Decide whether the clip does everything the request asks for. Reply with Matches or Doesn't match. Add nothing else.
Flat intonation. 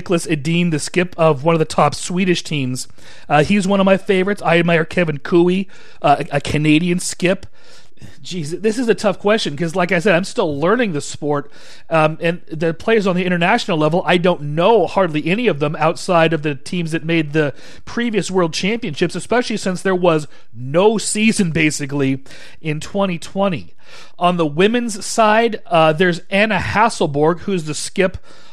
Doesn't match